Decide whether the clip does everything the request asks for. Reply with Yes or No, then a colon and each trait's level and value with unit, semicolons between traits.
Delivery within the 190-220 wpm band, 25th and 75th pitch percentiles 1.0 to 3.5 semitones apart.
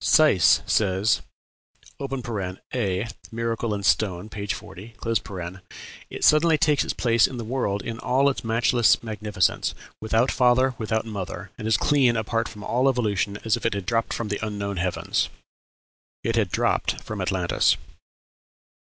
No: average, 145 wpm; average, 3.2 semitones